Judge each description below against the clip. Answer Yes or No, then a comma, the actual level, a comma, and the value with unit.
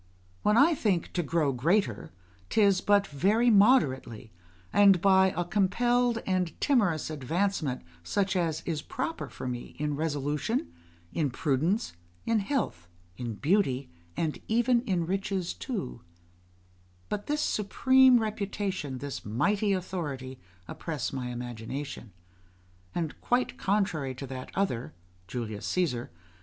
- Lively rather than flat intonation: Yes, wide, 7.5 semitones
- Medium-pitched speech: Yes, medium, 175 Hz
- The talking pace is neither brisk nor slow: No, slow, 125 wpm